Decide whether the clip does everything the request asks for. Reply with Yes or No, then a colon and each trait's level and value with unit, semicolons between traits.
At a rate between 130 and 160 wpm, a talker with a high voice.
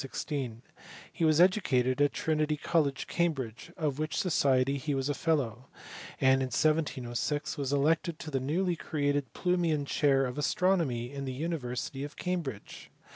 No: average, 145 wpm; medium, 145 Hz